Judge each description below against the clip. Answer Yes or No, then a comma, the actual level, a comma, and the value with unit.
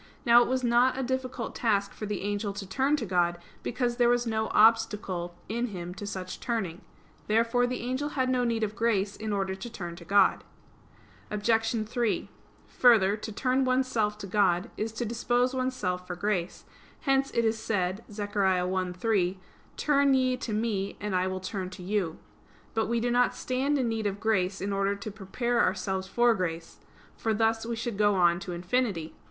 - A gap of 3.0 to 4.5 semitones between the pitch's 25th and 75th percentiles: Yes, average, 4.0 semitones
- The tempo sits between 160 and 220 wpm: Yes, average, 190 wpm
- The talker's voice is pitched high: Yes, high, 215 Hz